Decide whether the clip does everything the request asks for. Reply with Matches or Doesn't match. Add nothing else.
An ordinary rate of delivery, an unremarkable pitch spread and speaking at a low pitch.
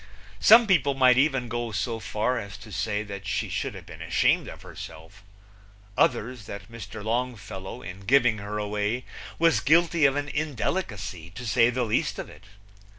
Matches